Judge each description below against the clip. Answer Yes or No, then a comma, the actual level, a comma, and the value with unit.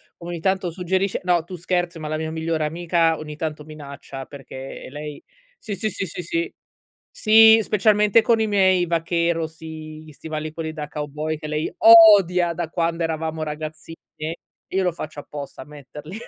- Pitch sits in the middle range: Yes, medium, 165 Hz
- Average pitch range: Yes, average, 3.0 semitones